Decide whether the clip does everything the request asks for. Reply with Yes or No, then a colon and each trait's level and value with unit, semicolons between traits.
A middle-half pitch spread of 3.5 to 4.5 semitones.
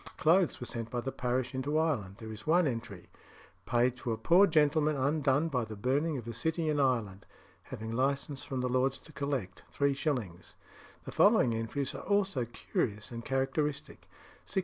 Yes: average, 4.2 semitones